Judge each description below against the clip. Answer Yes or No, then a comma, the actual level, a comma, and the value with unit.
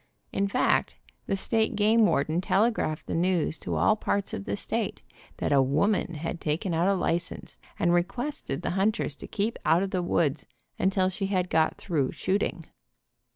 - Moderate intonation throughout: Yes, average, 3.7 semitones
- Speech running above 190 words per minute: No, average, 175 wpm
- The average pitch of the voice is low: No, medium, 185 Hz